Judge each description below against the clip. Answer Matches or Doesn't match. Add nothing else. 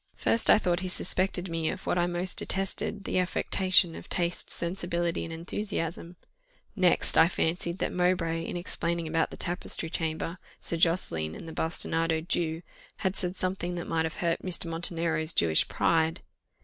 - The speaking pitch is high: Doesn't match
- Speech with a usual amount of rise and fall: Doesn't match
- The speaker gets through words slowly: Doesn't match